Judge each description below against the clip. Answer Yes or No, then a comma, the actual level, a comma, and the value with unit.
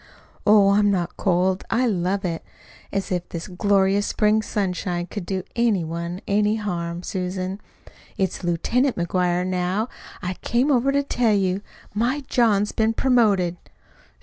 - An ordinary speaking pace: Yes, average, 145 wpm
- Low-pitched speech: No, high, 195 Hz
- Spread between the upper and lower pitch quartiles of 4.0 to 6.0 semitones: No, average, 3.3 semitones